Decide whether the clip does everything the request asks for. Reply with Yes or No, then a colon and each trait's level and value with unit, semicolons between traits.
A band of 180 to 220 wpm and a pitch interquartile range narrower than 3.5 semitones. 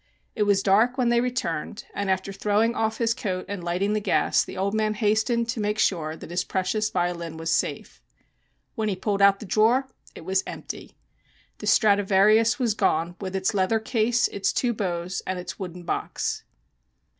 Yes: average, 185 wpm; average, 2.9 semitones